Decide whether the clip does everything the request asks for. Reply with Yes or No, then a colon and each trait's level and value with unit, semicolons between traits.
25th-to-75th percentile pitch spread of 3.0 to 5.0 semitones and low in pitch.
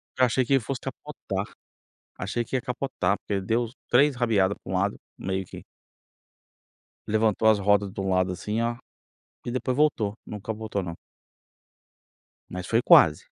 Yes: average, 3.9 semitones; low, 110 Hz